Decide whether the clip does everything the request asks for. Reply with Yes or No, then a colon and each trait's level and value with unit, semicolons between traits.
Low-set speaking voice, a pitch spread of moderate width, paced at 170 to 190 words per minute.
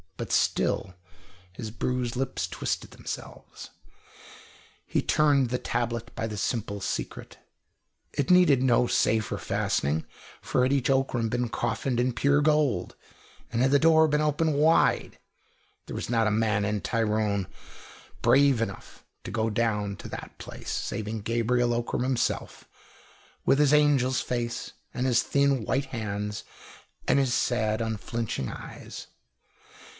No: low, 120 Hz; average, 3.7 semitones; average, 140 wpm